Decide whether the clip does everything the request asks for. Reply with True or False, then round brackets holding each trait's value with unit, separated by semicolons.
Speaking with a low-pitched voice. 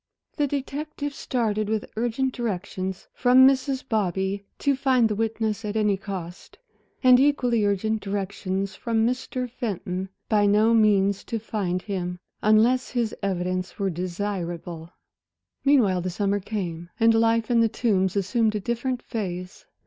False (215 Hz)